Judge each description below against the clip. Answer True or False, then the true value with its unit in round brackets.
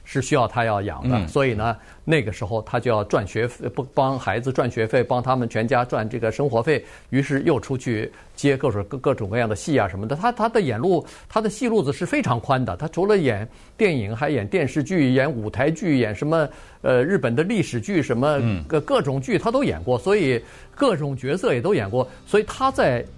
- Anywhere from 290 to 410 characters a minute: True (315 characters per minute)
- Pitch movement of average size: True (4.7 semitones)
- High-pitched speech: False (135 Hz)